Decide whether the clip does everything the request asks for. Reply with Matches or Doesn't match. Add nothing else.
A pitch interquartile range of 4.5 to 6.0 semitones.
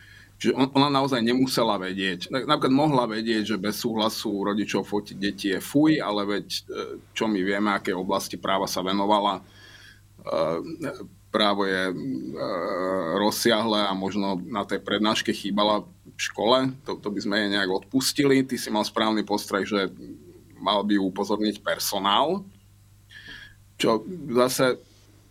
Doesn't match